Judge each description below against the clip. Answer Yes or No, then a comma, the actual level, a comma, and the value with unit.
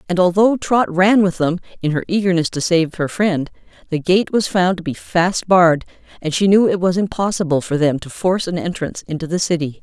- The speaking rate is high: Yes, fast, 220 wpm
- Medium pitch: Yes, medium, 175 Hz